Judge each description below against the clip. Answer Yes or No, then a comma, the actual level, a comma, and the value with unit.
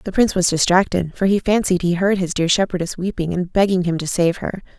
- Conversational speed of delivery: No, fast, 240 wpm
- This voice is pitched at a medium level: Yes, medium, 180 Hz